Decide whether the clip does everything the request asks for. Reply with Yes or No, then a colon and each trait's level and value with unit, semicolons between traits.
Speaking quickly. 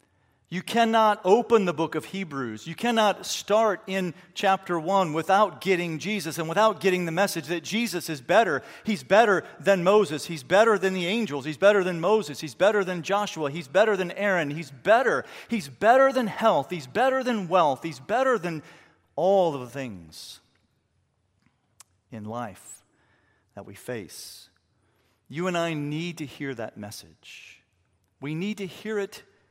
No: average, 165 wpm